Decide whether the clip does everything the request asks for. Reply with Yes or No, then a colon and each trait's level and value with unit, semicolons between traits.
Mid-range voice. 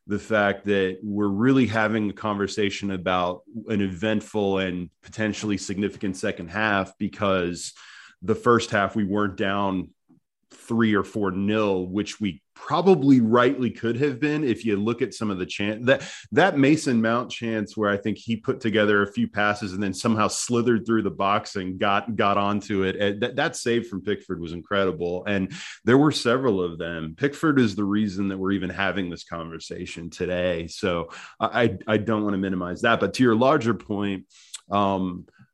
No: low, 105 Hz